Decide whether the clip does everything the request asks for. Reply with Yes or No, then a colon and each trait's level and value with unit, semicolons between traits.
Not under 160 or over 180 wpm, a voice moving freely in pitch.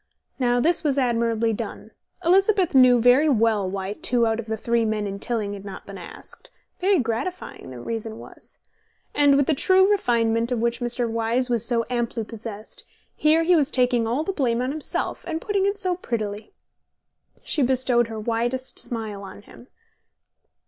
No: average, 175 wpm; average, 4.0 semitones